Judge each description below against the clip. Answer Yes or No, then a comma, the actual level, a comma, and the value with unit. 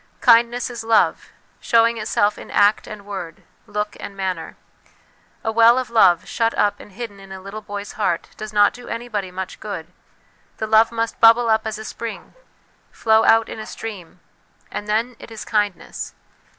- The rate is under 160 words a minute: No, average, 175 wpm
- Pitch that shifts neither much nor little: No, narrow, 2.1 semitones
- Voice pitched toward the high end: Yes, high, 215 Hz